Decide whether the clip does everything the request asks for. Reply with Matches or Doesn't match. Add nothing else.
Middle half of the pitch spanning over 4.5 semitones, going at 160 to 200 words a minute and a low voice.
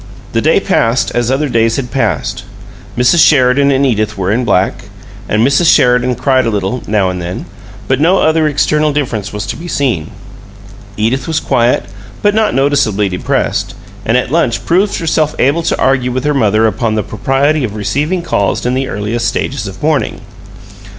Matches